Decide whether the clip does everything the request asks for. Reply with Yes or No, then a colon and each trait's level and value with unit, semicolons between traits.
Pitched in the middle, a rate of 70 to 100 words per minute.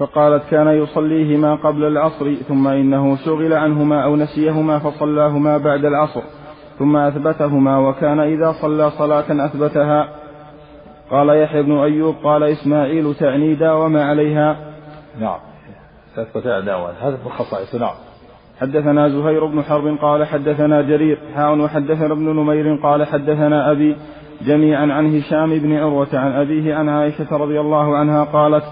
No: medium, 150 Hz; average, 125 wpm